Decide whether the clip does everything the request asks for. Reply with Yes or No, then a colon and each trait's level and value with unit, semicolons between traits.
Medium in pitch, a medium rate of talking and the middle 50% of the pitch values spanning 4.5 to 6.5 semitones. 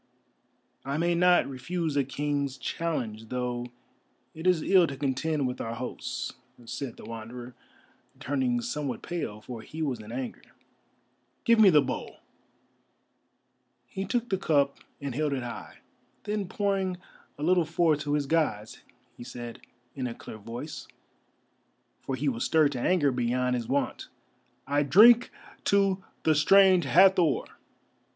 Yes: medium, 145 Hz; average, 145 wpm; wide, 5.5 semitones